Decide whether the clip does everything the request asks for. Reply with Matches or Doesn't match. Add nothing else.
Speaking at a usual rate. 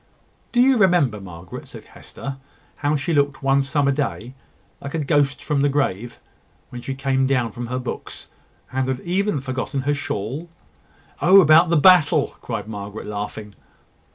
Matches